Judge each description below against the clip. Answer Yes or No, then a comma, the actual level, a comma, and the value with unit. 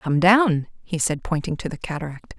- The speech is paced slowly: No, average, 200 wpm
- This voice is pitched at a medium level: Yes, medium, 170 Hz